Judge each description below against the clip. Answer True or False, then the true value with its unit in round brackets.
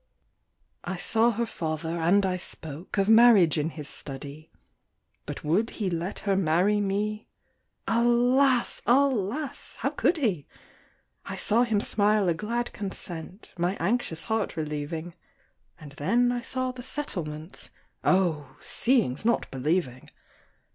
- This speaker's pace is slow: True (130 wpm)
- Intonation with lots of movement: True (6.4 semitones)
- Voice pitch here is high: True (195 Hz)